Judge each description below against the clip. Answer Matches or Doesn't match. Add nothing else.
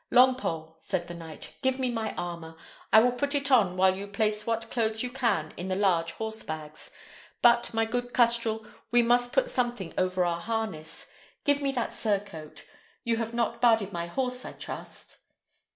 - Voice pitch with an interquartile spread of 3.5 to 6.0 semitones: Matches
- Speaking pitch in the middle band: Doesn't match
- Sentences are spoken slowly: Doesn't match